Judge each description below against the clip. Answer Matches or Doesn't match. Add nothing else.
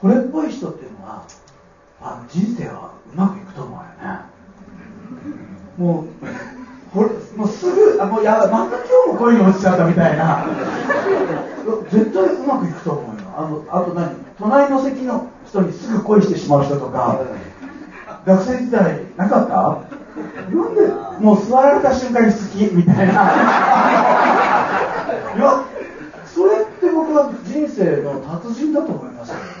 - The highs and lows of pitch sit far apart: Matches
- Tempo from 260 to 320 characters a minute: Matches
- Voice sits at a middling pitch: Doesn't match